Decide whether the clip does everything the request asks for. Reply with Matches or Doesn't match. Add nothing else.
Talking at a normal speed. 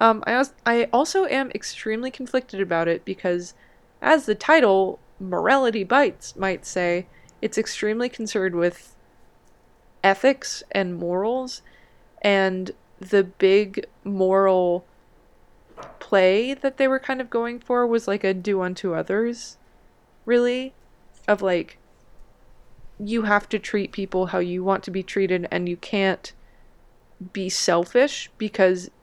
Doesn't match